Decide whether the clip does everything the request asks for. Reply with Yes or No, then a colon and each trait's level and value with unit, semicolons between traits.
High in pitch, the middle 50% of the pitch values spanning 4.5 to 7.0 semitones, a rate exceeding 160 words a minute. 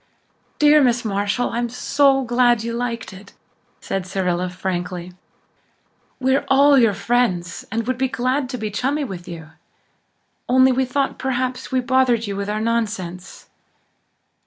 No: high, 235 Hz; average, 4.8 semitones; average, 145 wpm